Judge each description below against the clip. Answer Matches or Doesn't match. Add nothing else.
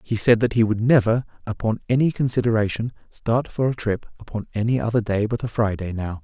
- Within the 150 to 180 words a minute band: Doesn't match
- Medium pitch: Doesn't match